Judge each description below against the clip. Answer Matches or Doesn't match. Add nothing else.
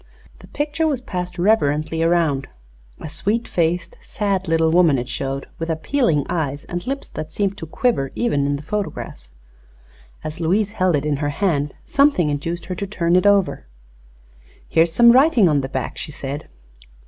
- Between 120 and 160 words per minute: Doesn't match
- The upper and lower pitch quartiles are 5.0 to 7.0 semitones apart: Matches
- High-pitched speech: Doesn't match